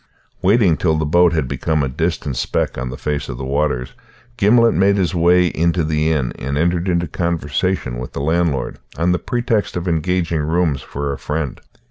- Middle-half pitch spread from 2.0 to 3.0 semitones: No, average, 3.7 semitones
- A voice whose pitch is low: Yes, very low, 80 Hz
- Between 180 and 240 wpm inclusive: Yes, average, 190 wpm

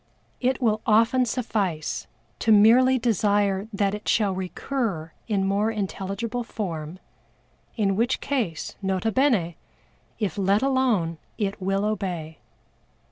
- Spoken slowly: Yes, slow, 120 wpm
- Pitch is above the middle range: Yes, high, 205 Hz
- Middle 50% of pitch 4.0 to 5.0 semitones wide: No, average, 3.4 semitones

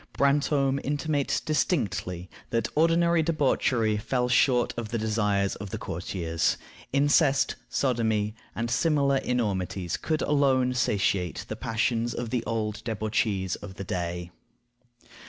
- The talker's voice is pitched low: Yes, low, 115 Hz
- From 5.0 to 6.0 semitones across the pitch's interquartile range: Yes, wide, 5.5 semitones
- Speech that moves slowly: Yes, slow, 120 wpm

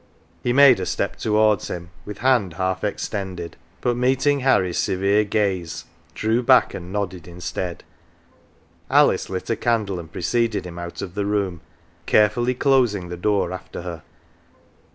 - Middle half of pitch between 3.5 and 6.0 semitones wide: Yes, average, 4.6 semitones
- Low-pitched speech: Yes, low, 100 Hz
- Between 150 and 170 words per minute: Yes, average, 155 wpm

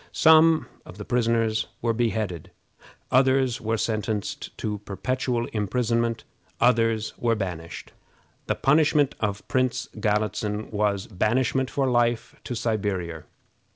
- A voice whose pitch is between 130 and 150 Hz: No, low, 115 Hz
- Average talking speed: No, slow, 115 wpm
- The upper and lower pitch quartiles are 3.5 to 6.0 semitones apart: No, average, 3.0 semitones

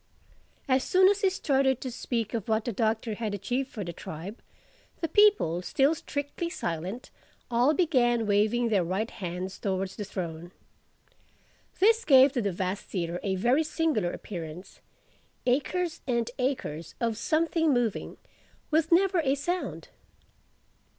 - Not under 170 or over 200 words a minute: No, average, 140 wpm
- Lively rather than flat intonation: Yes, wide, 7.4 semitones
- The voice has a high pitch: Yes, high, 240 Hz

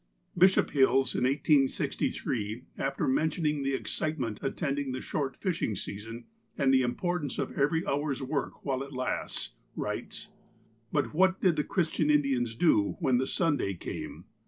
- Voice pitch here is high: No, medium, 140 Hz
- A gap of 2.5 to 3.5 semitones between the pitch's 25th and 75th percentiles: Yes, average, 3.2 semitones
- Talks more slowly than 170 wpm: Yes, average, 145 wpm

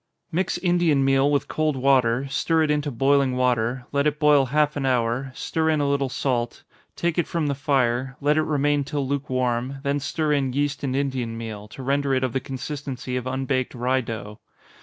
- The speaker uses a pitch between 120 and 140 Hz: Yes, low, 135 Hz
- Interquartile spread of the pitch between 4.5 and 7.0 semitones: No, narrow, 2.4 semitones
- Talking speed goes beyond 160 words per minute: Yes, average, 200 wpm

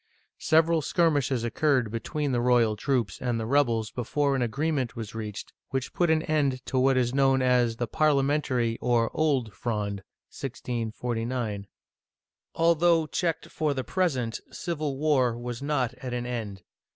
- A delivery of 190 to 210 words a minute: No, average, 155 wpm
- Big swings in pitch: No, average, 4.0 semitones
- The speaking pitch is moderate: No, low, 125 Hz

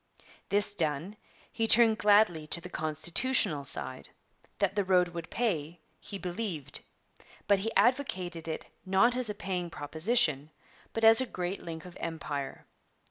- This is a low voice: No, medium, 180 Hz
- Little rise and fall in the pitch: No, average, 5.1 semitones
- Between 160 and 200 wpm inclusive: No, average, 145 wpm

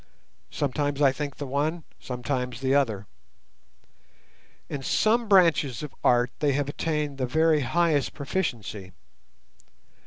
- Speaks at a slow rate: Yes, slow, 120 wpm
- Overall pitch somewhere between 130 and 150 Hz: Yes, medium, 140 Hz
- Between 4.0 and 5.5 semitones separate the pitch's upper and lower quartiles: No, average, 3.3 semitones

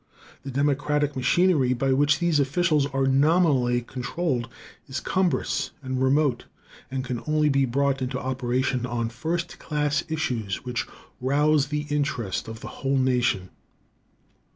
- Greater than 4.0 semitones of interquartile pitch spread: No, average, 2.9 semitones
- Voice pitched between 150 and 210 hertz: No, low, 135 Hz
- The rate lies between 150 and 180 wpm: No, slow, 135 wpm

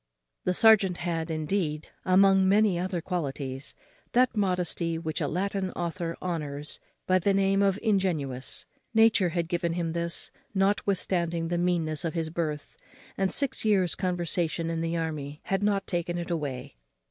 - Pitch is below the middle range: No, medium, 175 Hz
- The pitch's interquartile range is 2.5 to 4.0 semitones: Yes, average, 3.0 semitones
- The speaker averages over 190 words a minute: No, average, 150 wpm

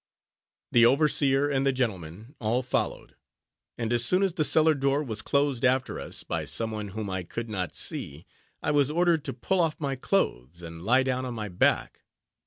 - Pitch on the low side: Yes, low, 125 Hz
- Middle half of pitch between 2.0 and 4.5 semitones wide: No, average, 5.0 semitones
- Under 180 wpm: No, average, 195 wpm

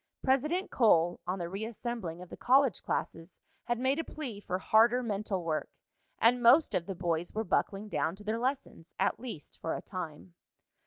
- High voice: Yes, high, 210 Hz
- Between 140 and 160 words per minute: No, average, 180 wpm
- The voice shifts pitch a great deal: Yes, wide, 5.8 semitones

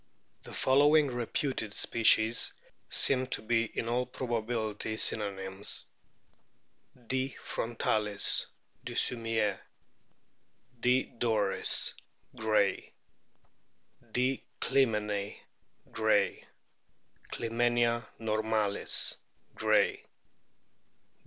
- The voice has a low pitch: Yes, low, 115 Hz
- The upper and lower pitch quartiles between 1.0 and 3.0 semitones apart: Yes, narrow, 2.5 semitones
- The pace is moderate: No, slow, 70 wpm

